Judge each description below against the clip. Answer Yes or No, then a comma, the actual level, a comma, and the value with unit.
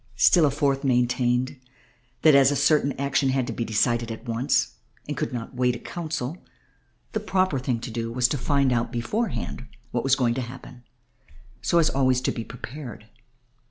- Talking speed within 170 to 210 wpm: Yes, average, 180 wpm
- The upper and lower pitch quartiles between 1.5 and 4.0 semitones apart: Yes, average, 2.8 semitones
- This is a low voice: Yes, low, 130 Hz